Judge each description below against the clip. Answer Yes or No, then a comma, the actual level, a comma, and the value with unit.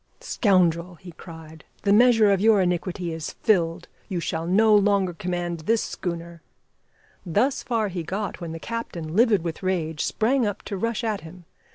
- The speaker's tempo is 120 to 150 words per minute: No, average, 175 wpm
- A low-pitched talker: No, medium, 185 Hz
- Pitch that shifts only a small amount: No, average, 4.0 semitones